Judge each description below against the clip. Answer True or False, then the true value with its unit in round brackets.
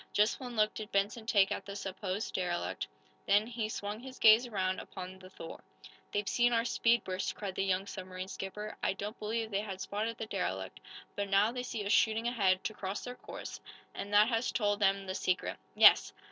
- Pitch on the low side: False (205 Hz)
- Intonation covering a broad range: False (2.7 semitones)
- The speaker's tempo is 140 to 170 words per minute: False (205 wpm)